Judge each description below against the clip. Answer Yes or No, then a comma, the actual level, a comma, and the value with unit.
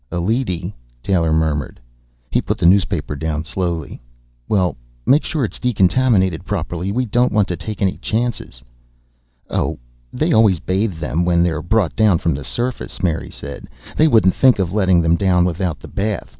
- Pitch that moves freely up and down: No, average, 4.3 semitones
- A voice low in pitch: Yes, very low, 95 Hz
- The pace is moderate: Yes, average, 170 wpm